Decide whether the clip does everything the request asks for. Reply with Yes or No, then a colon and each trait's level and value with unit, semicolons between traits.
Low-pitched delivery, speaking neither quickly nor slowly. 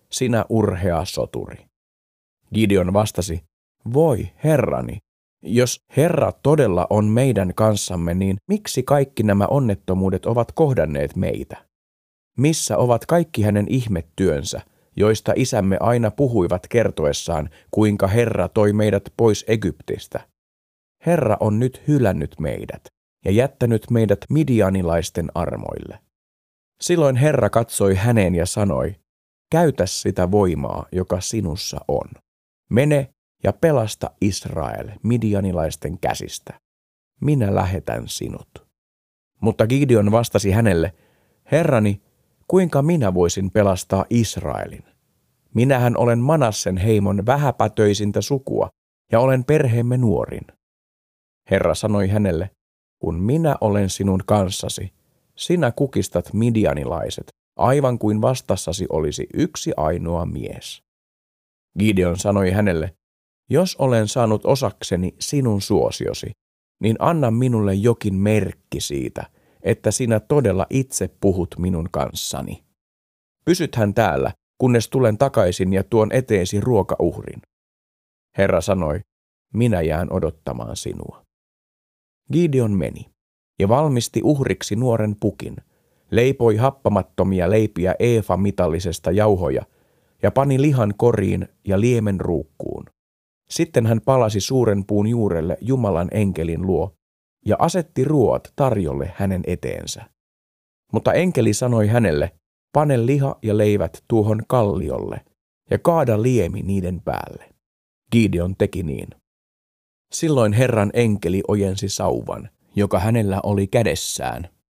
Yes: low, 105 Hz; average, 105 wpm